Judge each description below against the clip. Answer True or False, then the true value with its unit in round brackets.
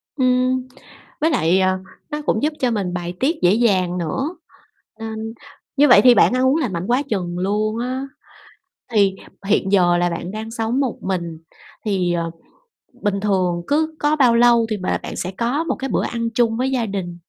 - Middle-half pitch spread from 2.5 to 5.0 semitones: False (5.4 semitones)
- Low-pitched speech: False (220 Hz)